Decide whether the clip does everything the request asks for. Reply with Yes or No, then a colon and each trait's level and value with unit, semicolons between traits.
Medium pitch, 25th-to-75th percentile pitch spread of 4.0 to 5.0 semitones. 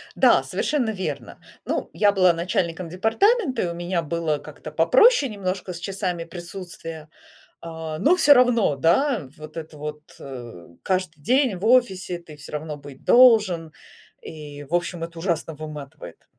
Yes: medium, 170 Hz; average, 4.5 semitones